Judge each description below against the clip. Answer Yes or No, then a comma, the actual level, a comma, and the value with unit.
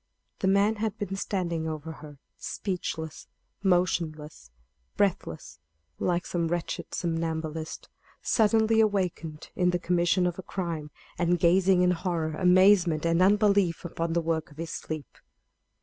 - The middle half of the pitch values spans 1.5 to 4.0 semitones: Yes, average, 2.9 semitones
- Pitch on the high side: No, medium, 175 Hz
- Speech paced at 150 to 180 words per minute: No, slow, 135 wpm